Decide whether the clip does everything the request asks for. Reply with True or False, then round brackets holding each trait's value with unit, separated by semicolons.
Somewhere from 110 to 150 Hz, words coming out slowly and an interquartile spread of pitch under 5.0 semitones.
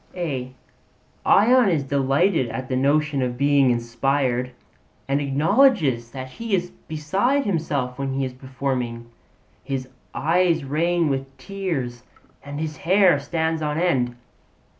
True (140 Hz; 120 wpm; 4.5 semitones)